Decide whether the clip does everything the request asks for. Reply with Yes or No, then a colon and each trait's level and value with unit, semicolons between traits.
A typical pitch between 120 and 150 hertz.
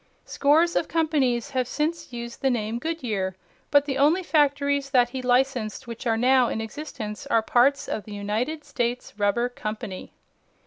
No: very high, 250 Hz